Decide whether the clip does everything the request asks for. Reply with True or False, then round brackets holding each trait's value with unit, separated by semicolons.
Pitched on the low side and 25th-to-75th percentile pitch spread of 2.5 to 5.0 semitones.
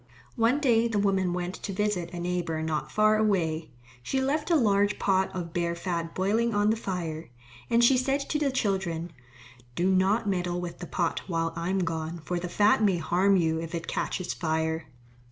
False (185 Hz; 4.0 semitones)